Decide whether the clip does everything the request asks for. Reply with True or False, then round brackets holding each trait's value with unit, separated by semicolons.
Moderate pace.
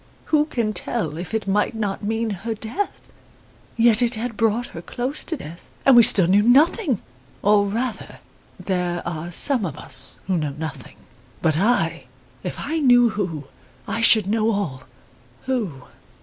True (165 wpm)